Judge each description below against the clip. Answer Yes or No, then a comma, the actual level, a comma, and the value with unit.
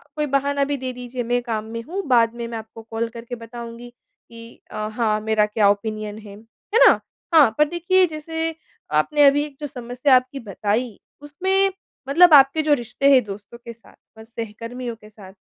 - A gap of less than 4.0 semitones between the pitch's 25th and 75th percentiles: No, average, 4.3 semitones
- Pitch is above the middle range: Yes, high, 240 Hz